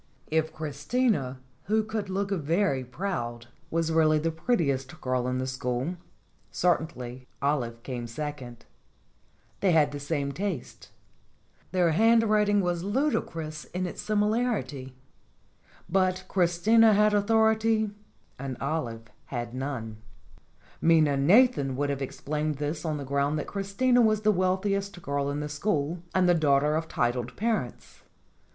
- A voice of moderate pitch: Yes, medium, 160 Hz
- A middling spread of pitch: No, wide, 6.4 semitones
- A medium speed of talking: No, slow, 130 wpm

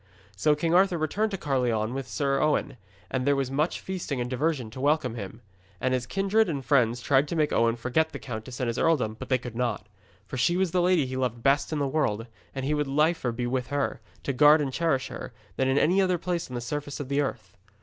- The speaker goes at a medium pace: No, fast, 240 wpm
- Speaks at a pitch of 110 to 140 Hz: Yes, low, 135 Hz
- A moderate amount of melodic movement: Yes, average, 3.9 semitones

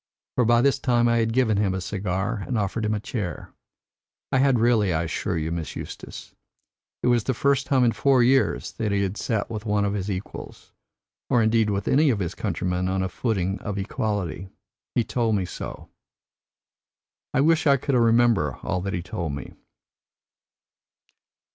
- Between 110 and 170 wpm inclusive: No, average, 185 wpm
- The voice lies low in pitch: Yes, low, 105 Hz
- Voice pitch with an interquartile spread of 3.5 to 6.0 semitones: Yes, average, 4.2 semitones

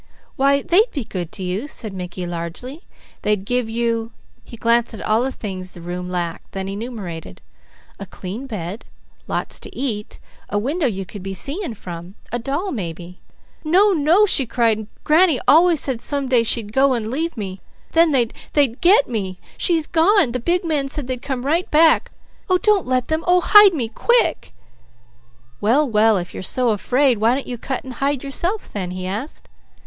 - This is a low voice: No, high, 245 Hz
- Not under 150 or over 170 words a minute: No, average, 185 wpm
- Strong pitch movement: Yes, wide, 6.8 semitones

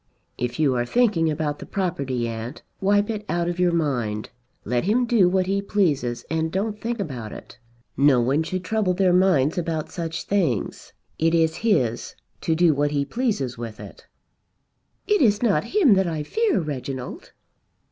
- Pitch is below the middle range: No, medium, 165 Hz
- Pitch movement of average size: No, wide, 6.5 semitones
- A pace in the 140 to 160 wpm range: No, average, 175 wpm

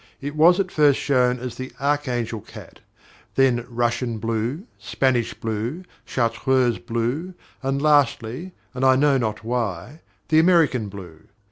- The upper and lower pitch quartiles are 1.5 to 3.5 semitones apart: No, average, 4.0 semitones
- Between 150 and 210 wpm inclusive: No, slow, 135 wpm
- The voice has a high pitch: No, low, 125 Hz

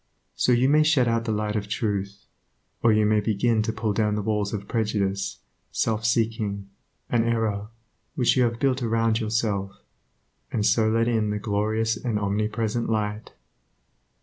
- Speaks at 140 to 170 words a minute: Yes, average, 165 wpm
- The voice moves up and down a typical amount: No, narrow, 1.7 semitones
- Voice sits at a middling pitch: No, low, 110 Hz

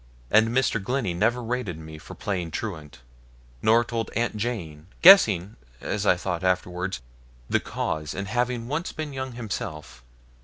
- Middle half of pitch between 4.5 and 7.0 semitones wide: Yes, wide, 5.6 semitones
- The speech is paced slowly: No, average, 150 wpm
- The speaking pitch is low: Yes, low, 105 Hz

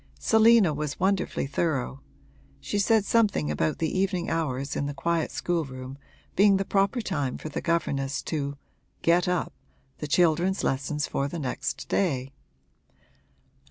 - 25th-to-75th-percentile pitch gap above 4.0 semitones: Yes, wide, 5.5 semitones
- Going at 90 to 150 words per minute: Yes, average, 140 wpm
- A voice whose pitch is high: No, medium, 160 Hz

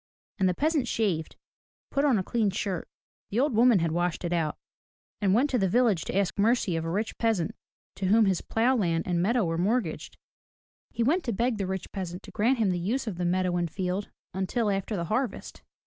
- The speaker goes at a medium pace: No, fast, 225 wpm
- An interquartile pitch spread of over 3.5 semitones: Yes, average, 4.7 semitones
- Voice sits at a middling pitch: No, high, 195 Hz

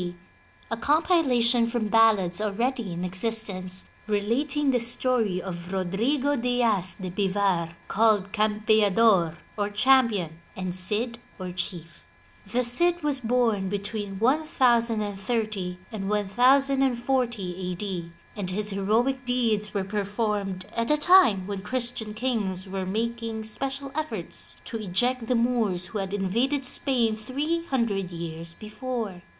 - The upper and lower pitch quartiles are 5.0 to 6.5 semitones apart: No, average, 4.4 semitones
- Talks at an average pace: No, slow, 125 wpm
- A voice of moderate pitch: No, high, 215 Hz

